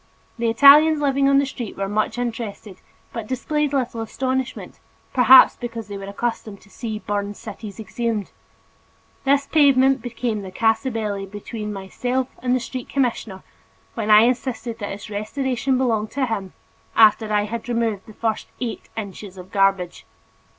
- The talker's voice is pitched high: Yes, high, 230 Hz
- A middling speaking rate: Yes, average, 155 wpm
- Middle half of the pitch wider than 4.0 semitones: No, average, 3.6 semitones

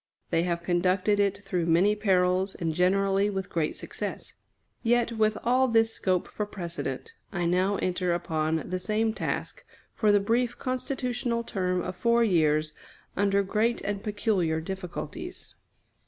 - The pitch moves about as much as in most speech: Yes, average, 3.6 semitones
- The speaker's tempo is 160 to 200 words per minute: No, average, 145 wpm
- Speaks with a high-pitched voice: Yes, high, 195 Hz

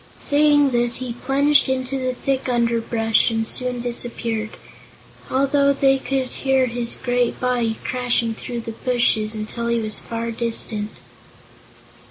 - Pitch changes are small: Yes, narrow, 2.3 semitones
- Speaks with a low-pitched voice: No, high, 245 Hz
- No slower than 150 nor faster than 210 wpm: No, slow, 135 wpm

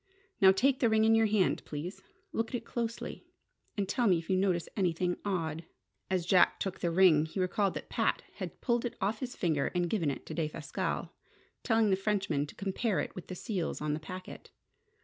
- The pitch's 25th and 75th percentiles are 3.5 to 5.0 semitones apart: Yes, average, 4.4 semitones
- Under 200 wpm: No, fast, 205 wpm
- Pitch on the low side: No, high, 190 Hz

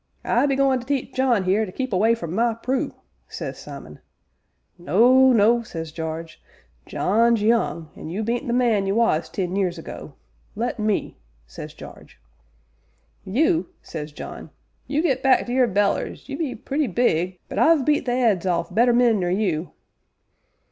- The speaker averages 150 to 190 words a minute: Yes, average, 170 wpm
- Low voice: No, high, 225 Hz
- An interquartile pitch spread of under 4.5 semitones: No, wide, 5.5 semitones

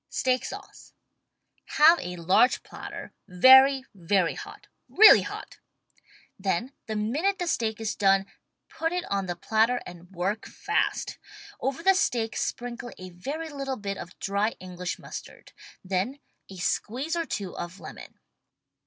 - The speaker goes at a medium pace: Yes, average, 145 wpm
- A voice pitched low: No, high, 220 Hz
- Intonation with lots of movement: Yes, wide, 6.4 semitones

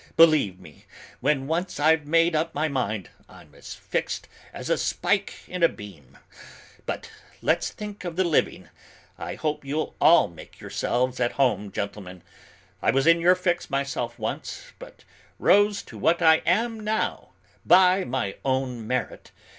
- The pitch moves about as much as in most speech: No, wide, 6.4 semitones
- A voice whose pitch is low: No, medium, 150 Hz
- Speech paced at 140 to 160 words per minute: Yes, average, 155 wpm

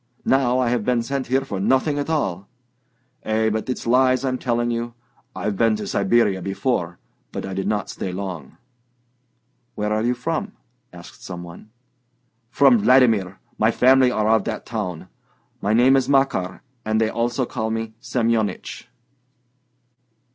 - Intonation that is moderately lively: Yes, average, 4.1 semitones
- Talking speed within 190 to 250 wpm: No, average, 155 wpm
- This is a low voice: Yes, low, 115 Hz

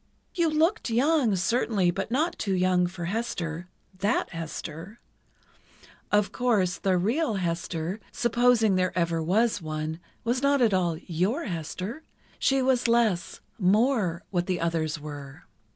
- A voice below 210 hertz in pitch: Yes, high, 190 Hz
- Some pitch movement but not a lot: No, wide, 5.7 semitones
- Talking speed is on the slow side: Yes, slow, 120 wpm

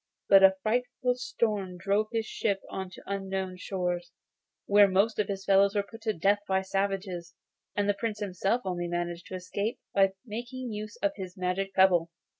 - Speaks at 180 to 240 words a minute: Yes, average, 185 wpm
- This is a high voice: Yes, high, 195 Hz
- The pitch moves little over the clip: Yes, narrow, 2.2 semitones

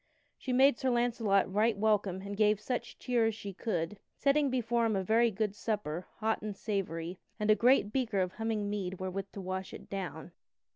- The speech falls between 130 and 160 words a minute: No, average, 195 wpm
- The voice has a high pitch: Yes, high, 210 Hz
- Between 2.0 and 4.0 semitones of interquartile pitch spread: Yes, average, 3.1 semitones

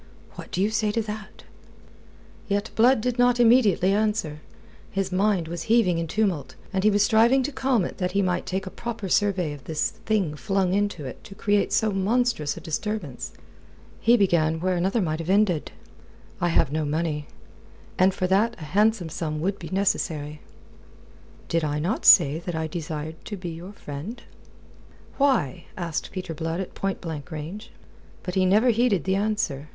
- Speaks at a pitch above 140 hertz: Yes, high, 190 Hz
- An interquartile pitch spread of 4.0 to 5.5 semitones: Yes, average, 4.7 semitones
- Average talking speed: Yes, average, 180 wpm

